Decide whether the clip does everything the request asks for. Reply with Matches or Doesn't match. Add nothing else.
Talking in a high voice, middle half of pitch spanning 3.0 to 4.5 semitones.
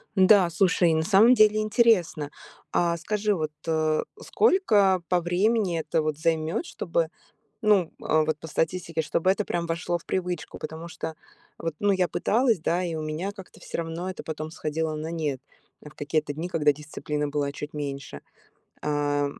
Doesn't match